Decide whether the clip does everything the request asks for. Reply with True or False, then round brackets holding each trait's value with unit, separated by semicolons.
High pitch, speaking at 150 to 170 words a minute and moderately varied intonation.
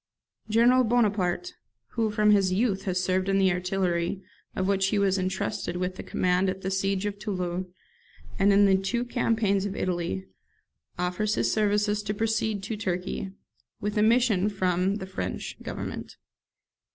False (195 Hz; 160 wpm; 2.2 semitones)